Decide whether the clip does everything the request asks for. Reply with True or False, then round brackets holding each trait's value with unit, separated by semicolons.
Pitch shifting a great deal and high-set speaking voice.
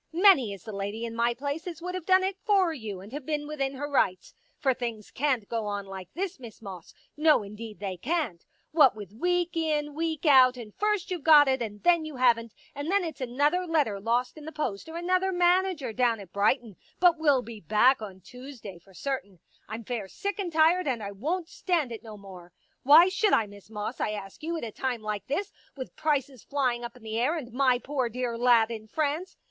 True (6.6 semitones; 255 Hz)